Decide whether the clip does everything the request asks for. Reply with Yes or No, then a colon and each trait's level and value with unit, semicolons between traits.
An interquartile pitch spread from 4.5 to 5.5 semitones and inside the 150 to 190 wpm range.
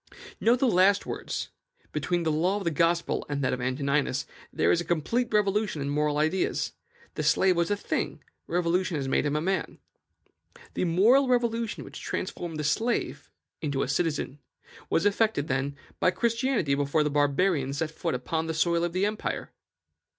Yes: average, 5.2 semitones; average, 175 wpm